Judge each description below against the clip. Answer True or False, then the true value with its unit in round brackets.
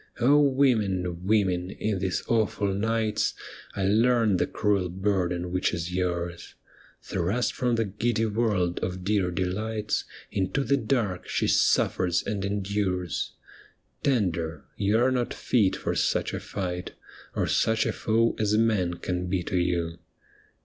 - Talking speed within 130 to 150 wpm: True (140 wpm)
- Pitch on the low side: True (100 Hz)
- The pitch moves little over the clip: False (3.8 semitones)